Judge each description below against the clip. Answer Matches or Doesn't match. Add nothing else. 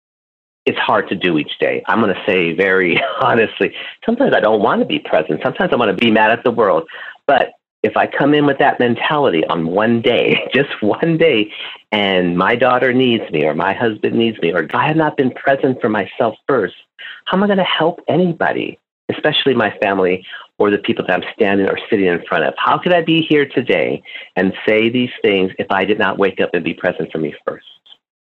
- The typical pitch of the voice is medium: Doesn't match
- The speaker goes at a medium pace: Doesn't match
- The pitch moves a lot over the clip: Matches